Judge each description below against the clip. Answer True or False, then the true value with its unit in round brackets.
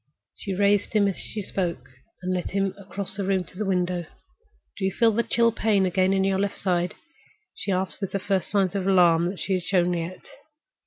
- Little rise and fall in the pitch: True (1.7 semitones)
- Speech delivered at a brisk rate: True (215 wpm)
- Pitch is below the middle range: False (190 Hz)